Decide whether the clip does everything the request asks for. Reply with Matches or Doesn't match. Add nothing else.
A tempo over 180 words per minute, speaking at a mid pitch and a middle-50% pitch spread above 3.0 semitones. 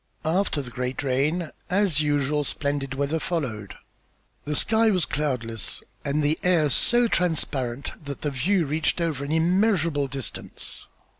Doesn't match